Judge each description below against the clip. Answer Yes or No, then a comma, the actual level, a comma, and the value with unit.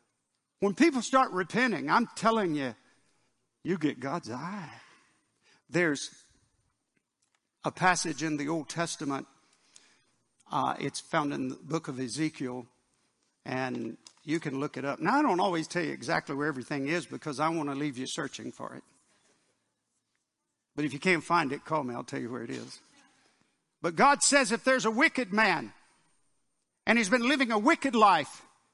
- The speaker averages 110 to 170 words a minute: Yes, average, 165 wpm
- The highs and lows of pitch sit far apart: Yes, wide, 7.9 semitones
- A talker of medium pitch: Yes, medium, 160 Hz